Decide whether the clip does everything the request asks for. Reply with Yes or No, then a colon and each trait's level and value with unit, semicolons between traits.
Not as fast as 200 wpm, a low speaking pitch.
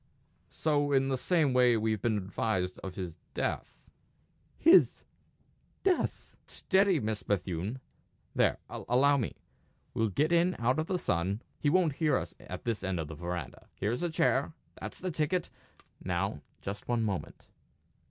Yes: average, 150 wpm; low, 125 Hz